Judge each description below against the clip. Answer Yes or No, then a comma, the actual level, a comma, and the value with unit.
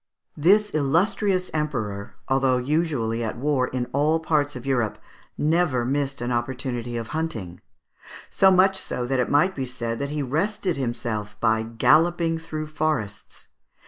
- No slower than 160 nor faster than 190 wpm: No, average, 150 wpm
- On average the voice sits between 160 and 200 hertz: No, medium, 140 Hz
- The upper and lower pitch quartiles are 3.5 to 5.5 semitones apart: Yes, average, 5.0 semitones